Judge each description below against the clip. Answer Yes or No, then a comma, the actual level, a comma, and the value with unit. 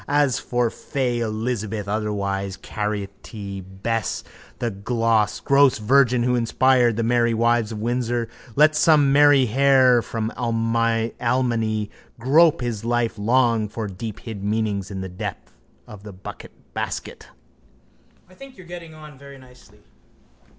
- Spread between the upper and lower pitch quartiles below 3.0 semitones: No, average, 3.4 semitones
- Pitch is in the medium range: No, low, 115 Hz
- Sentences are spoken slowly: Yes, slow, 120 wpm